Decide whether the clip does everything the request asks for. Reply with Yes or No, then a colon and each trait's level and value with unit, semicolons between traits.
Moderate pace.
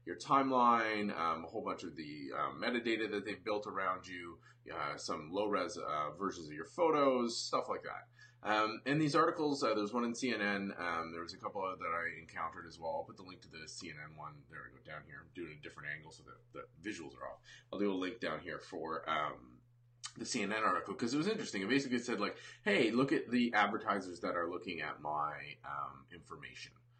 No: fast, 225 wpm